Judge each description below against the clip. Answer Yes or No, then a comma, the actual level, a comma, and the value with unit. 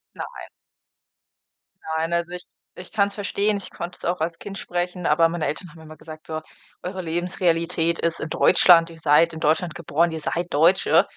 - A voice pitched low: No, medium, 170 Hz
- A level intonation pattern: Yes, narrow, 1.8 semitones